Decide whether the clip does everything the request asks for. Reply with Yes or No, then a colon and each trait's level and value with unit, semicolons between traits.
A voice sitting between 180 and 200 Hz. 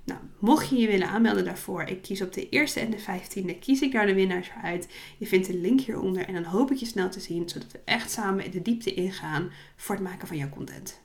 Yes: high, 190 Hz